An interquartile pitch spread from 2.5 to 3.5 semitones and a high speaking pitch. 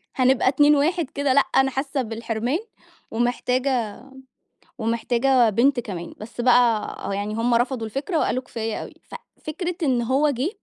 Yes: average, 3.2 semitones; very high, 250 Hz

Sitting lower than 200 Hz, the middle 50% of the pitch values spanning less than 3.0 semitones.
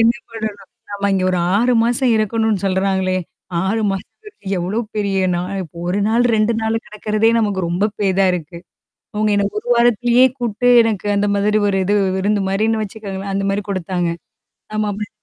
No: high, 205 Hz; narrow, 2.4 semitones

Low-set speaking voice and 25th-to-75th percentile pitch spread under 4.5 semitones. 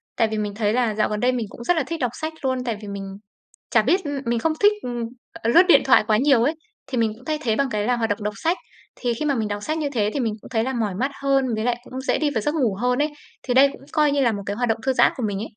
No: high, 245 Hz; average, 4.1 semitones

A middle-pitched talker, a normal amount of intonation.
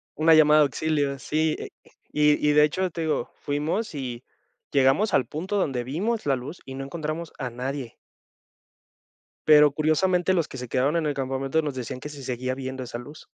Yes: medium, 145 Hz; average, 3.0 semitones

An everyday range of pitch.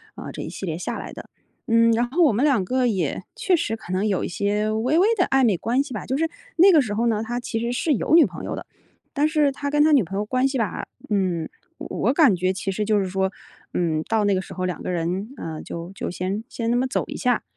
No: wide, 5.9 semitones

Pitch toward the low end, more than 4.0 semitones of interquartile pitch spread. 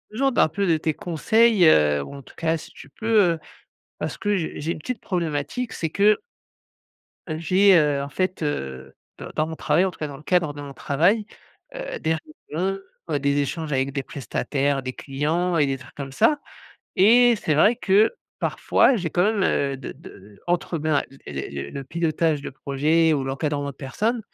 No: medium, 155 Hz; average, 5.2 semitones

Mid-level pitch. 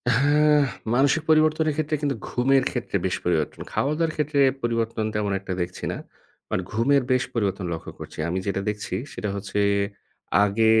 No: low, 125 Hz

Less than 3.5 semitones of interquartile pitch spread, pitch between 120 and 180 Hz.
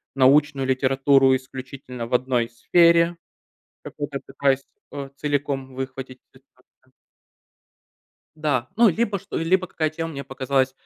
Yes: narrow, 2.5 semitones; low, 135 Hz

